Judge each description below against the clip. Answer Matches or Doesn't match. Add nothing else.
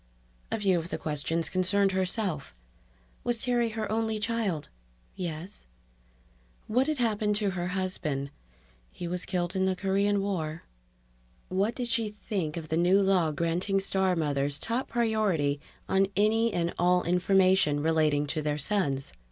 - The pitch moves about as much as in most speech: Matches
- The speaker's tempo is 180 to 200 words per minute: Doesn't match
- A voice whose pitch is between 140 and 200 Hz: Matches